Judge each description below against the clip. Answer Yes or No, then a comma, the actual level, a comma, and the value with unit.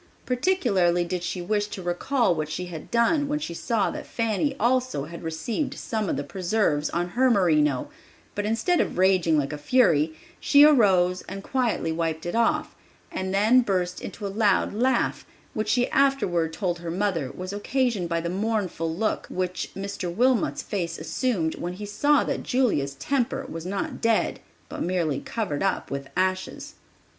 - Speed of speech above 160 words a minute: Yes, average, 170 wpm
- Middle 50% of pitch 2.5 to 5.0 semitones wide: No, wide, 5.4 semitones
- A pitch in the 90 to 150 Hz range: No, high, 195 Hz